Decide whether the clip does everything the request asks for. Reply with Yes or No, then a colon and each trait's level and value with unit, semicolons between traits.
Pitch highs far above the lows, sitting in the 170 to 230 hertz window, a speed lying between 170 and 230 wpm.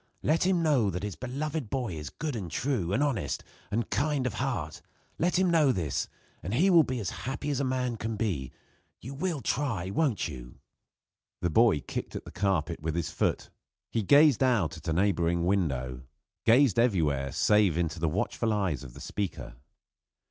No: wide, 8.0 semitones; low, 105 Hz; average, 185 wpm